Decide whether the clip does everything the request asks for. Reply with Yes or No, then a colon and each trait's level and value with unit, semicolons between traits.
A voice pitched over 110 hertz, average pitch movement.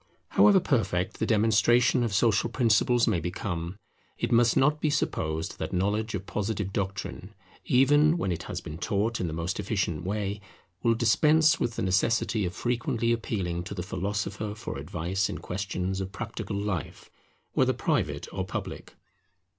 No: low, 105 Hz; average, 3.9 semitones